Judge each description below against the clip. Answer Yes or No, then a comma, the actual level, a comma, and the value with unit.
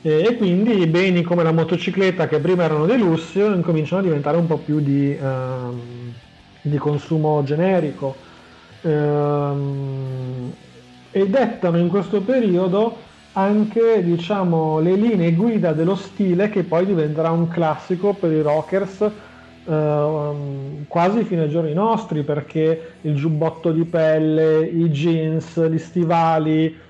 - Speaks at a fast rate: No, average, 130 wpm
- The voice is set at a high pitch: No, medium, 165 Hz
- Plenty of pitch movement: No, average, 3.7 semitones